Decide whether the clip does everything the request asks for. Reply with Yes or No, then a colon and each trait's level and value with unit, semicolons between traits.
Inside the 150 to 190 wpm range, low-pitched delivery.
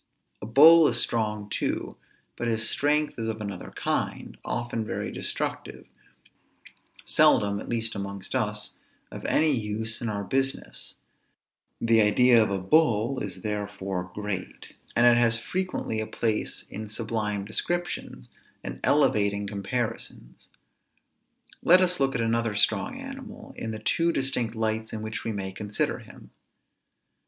No: average, 140 wpm; low, 110 Hz